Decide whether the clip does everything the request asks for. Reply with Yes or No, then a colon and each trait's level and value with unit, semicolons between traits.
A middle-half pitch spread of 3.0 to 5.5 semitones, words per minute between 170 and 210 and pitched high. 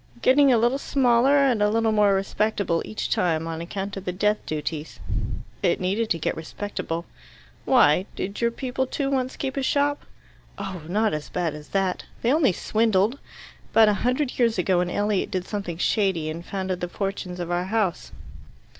Yes: average, 4.7 semitones; average, 180 wpm; high, 205 Hz